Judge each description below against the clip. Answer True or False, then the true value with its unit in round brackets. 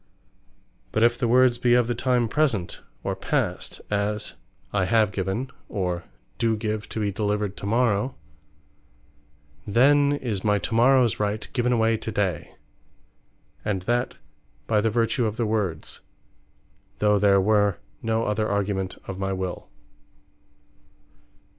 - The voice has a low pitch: True (110 Hz)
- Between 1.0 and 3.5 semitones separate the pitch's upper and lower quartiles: True (2.9 semitones)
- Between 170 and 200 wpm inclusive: False (140 wpm)